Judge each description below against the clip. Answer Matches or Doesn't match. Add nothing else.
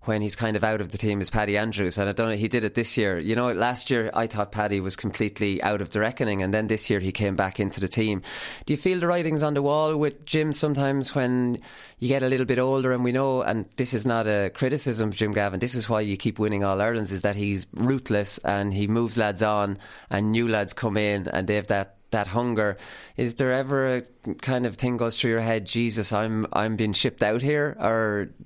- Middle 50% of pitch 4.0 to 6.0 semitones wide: Doesn't match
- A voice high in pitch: Doesn't match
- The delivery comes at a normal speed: Doesn't match